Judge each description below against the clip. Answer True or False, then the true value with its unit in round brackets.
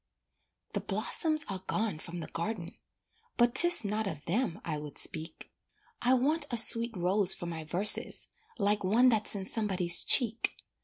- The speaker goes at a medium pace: True (160 wpm)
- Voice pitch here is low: False (205 Hz)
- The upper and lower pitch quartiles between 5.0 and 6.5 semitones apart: True (5.4 semitones)